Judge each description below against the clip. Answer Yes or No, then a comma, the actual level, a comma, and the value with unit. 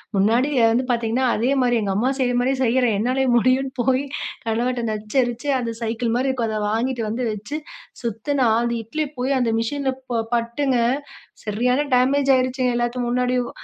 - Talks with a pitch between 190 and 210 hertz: No, high, 245 Hz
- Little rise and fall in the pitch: Yes, narrow, 2.2 semitones